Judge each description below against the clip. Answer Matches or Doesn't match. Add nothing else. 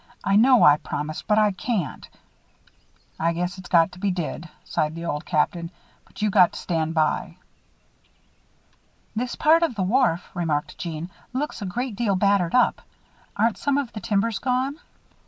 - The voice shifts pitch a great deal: Matches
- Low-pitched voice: Doesn't match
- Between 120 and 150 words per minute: Doesn't match